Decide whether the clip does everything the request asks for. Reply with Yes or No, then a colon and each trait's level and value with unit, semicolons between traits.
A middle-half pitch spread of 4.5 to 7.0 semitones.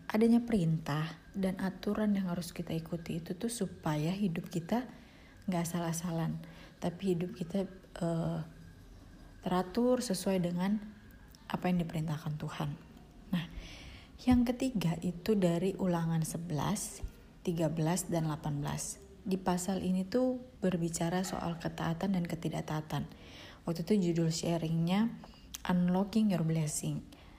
No: average, 2.9 semitones